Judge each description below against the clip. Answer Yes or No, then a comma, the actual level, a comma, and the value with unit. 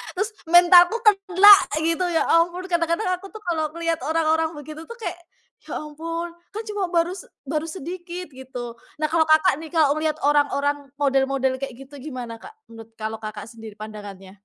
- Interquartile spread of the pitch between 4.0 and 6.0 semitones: Yes, average, 4.6 semitones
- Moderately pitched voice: No, very high, 315 Hz